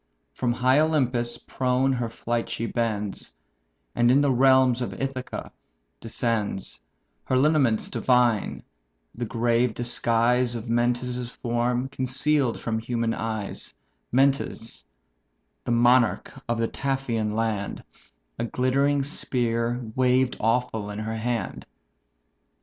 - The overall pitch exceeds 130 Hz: No, low, 120 Hz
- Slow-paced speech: Yes, slow, 115 wpm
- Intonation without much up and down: Yes, narrow, 1.9 semitones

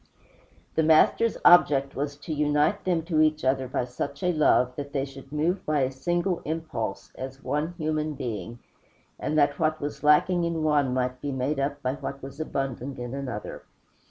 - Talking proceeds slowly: No, average, 185 wpm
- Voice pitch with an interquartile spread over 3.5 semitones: No, average, 2.8 semitones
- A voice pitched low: No, medium, 145 Hz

